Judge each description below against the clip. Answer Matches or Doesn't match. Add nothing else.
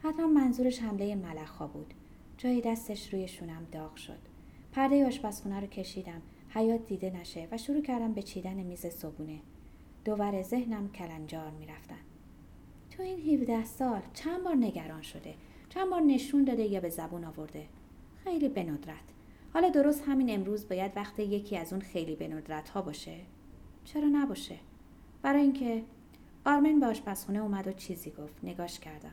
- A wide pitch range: Matches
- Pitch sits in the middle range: Doesn't match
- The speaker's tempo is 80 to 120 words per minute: Doesn't match